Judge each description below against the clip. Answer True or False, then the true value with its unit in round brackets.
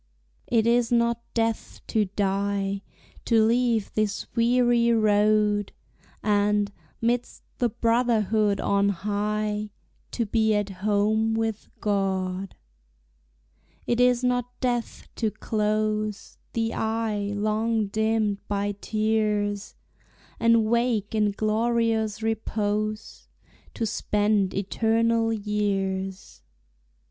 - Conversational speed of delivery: False (95 wpm)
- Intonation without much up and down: True (1.8 semitones)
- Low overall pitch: False (215 Hz)